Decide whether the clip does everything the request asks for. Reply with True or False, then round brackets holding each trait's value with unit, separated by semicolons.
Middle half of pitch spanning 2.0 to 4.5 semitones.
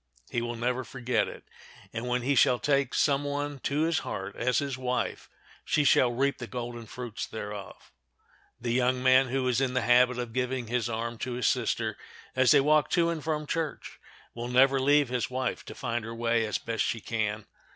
True (2.5 semitones)